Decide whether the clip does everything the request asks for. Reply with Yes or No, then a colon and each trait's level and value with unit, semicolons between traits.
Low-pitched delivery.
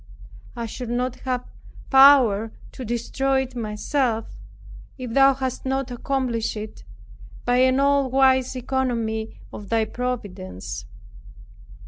No: very high, 250 Hz